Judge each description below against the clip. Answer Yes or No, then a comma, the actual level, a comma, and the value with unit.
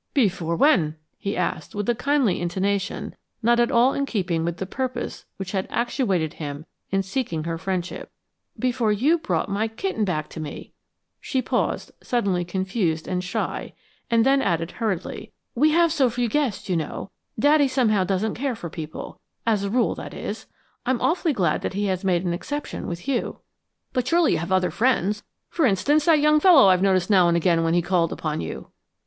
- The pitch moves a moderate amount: No, wide, 6.5 semitones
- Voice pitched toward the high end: Yes, high, 200 Hz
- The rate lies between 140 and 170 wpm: No, average, 190 wpm